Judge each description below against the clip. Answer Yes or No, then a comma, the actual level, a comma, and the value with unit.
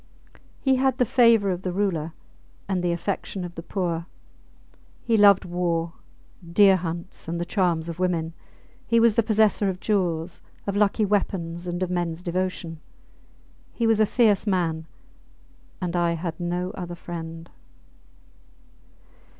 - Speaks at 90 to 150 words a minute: Yes, average, 145 wpm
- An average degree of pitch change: Yes, average, 3.1 semitones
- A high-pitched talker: No, medium, 180 Hz